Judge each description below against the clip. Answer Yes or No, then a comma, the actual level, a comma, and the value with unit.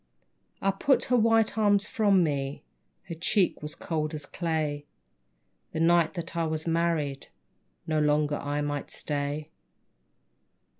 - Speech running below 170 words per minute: Yes, slow, 135 wpm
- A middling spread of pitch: Yes, average, 3.8 semitones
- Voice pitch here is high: No, medium, 160 Hz